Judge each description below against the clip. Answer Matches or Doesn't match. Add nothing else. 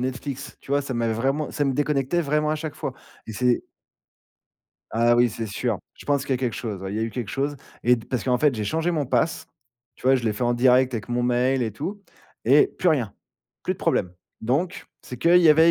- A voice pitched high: Doesn't match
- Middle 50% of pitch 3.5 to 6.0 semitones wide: Matches